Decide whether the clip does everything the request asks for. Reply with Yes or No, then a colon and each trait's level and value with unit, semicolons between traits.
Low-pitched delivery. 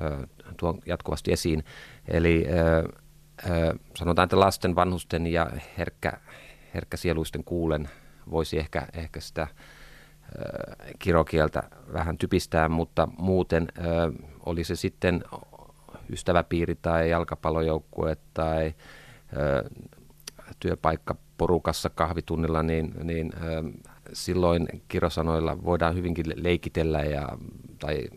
Yes: very low, 85 Hz